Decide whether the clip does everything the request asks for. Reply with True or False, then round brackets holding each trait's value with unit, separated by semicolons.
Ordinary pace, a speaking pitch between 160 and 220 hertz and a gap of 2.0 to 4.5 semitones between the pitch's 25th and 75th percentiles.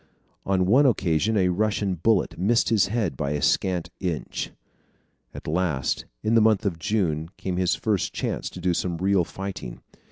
False (170 wpm; 95 Hz; 3.8 semitones)